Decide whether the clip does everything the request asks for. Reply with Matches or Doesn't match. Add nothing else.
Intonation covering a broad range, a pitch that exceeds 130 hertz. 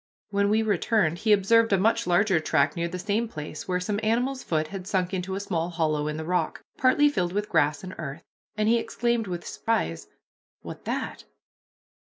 Doesn't match